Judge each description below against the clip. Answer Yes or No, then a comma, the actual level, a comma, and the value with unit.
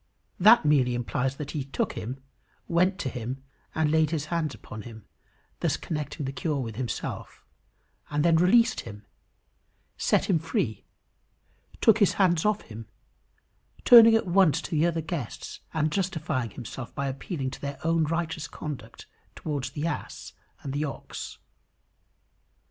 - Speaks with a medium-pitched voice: Yes, medium, 150 Hz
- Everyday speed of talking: Yes, average, 150 wpm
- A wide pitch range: No, average, 4.5 semitones